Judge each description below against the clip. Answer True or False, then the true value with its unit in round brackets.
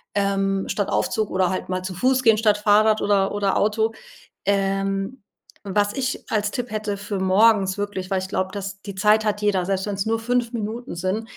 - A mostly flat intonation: True (1.9 semitones)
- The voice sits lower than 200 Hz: False (205 Hz)